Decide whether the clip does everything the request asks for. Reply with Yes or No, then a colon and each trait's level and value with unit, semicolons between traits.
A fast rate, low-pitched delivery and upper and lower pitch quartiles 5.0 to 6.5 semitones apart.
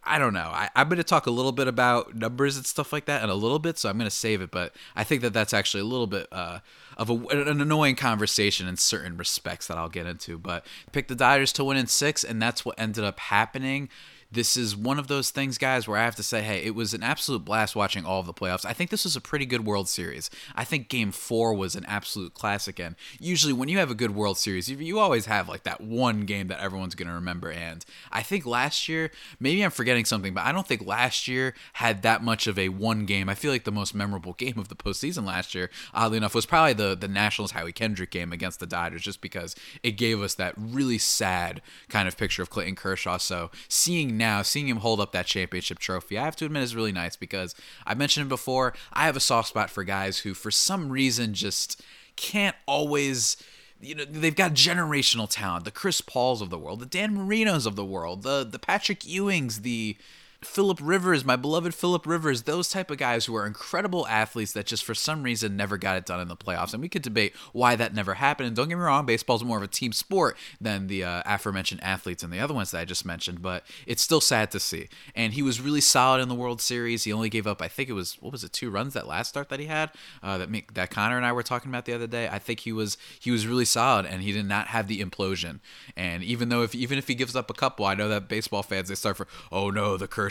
Yes: fast, 255 wpm; low, 115 Hz; average, 5.3 semitones